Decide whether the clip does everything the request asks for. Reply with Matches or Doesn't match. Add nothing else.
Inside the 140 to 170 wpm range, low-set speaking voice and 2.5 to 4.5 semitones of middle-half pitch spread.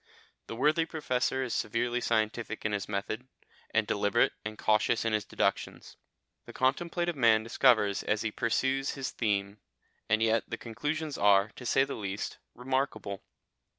Matches